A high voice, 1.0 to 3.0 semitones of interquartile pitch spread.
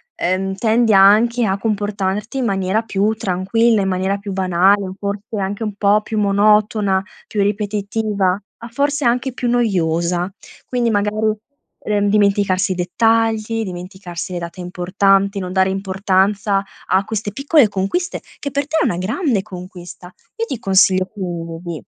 Yes: high, 200 Hz; narrow, 2.6 semitones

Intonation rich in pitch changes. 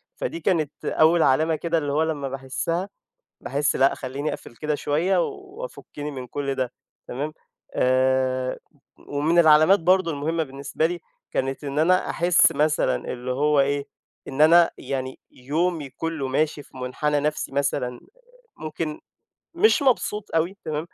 No: average, 3.4 semitones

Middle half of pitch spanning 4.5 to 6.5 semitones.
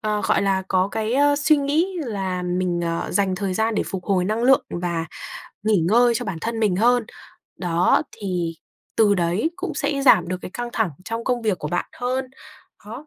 Yes: average, 5.0 semitones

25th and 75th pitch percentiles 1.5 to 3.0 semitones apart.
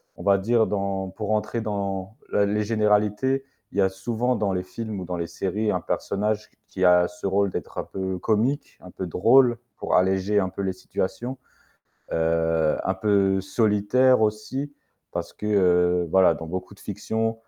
Yes: average, 2.7 semitones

